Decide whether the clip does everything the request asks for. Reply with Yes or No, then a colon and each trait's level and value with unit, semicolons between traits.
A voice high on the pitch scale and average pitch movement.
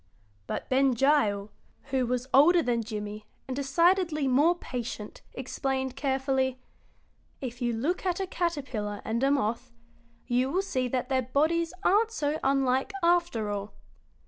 Yes: very high, 265 Hz; average, 4.0 semitones